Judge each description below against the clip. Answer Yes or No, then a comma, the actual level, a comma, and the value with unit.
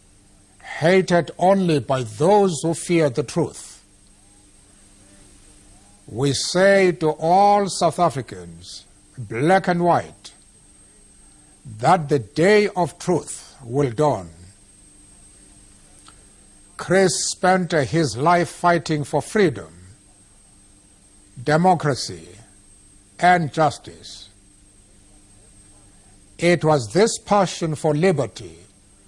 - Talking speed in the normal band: No, slow, 85 wpm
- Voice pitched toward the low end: Yes, low, 120 Hz